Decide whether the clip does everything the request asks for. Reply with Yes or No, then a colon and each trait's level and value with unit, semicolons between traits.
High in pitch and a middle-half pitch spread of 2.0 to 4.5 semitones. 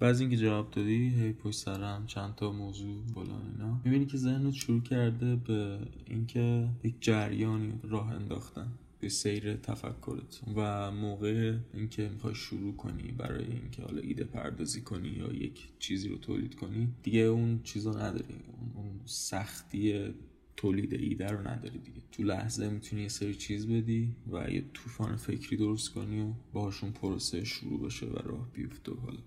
No: low, 110 Hz; narrow, 2.4 semitones